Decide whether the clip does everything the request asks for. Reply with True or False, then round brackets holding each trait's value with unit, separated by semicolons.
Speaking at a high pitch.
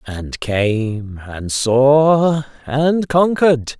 False (135 Hz)